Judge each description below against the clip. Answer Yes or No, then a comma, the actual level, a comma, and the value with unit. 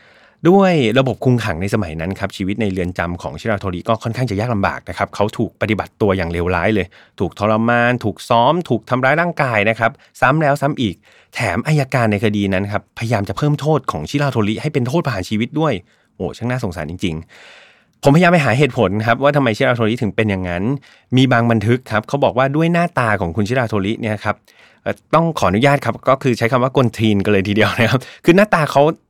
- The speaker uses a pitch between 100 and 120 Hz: Yes, low, 115 Hz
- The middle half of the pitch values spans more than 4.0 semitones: Yes, average, 4.7 semitones